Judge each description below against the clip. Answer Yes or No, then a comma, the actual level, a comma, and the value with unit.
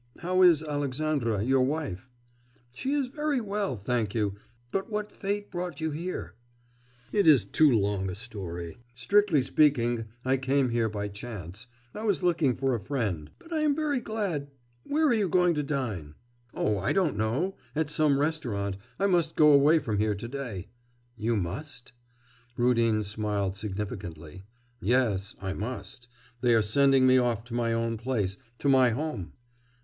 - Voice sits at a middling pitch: No, low, 125 Hz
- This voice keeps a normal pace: Yes, average, 165 wpm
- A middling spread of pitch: No, wide, 7.0 semitones